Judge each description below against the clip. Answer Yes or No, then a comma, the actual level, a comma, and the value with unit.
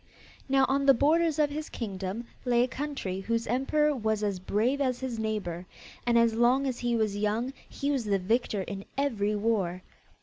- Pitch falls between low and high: No, high, 235 Hz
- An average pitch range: Yes, average, 4.6 semitones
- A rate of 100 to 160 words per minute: No, average, 190 wpm